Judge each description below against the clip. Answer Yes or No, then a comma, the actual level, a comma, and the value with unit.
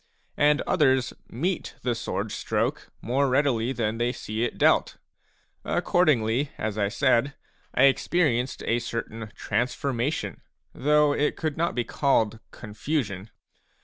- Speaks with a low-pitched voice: Yes, low, 125 Hz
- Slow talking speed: Yes, slow, 130 wpm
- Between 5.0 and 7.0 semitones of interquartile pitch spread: No, average, 4.2 semitones